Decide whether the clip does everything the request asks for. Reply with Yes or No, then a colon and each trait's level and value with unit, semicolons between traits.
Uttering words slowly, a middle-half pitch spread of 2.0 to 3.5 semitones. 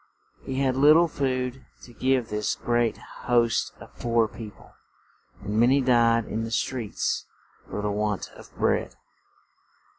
No: average, 155 wpm; average, 2.8 semitones